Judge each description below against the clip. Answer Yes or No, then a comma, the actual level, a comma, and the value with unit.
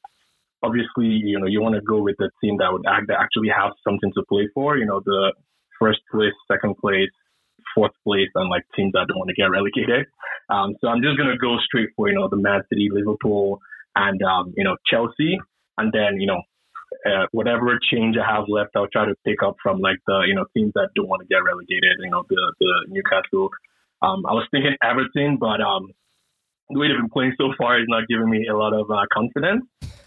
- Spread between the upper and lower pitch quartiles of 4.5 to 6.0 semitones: Yes, wide, 5.5 semitones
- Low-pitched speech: Yes, low, 110 Hz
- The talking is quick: Yes, fast, 225 wpm